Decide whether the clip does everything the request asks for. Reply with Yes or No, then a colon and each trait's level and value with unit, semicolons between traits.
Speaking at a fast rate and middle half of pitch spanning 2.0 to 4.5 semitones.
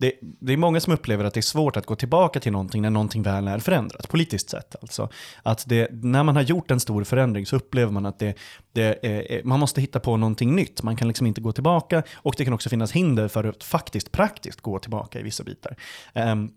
Yes: fast, 245 wpm; average, 4.1 semitones